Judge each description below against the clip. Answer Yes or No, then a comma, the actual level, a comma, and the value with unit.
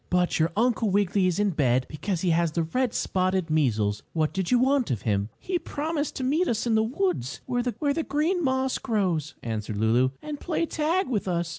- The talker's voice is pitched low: No, high, 195 Hz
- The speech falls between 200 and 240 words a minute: Yes, fast, 205 wpm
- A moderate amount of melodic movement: No, wide, 8.9 semitones